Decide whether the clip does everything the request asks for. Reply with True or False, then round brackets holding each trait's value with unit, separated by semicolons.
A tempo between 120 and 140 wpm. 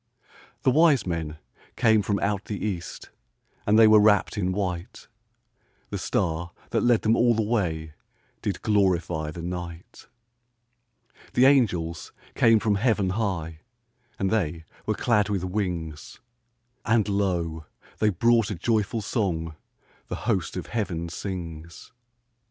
True (135 wpm)